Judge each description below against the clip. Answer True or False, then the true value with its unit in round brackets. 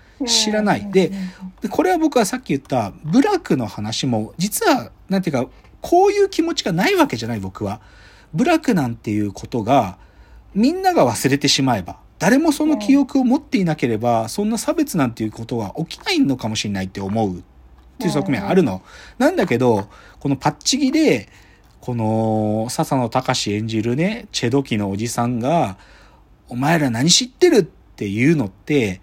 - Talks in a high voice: False (140 Hz)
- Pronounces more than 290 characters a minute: True (350 characters per minute)